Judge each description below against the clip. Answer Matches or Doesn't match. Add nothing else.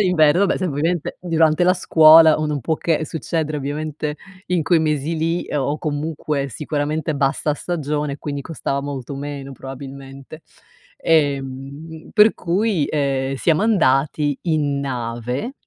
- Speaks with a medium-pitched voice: Matches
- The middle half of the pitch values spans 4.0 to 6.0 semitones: Doesn't match